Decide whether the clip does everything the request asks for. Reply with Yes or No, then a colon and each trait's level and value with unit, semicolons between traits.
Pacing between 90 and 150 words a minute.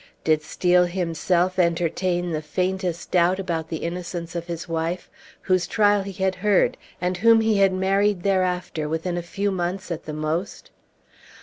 No: average, 165 wpm